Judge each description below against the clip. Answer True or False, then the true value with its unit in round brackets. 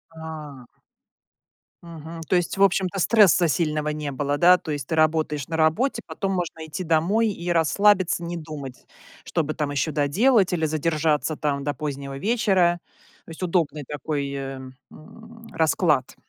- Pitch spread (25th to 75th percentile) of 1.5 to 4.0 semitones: True (3.2 semitones)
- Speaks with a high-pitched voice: False (160 Hz)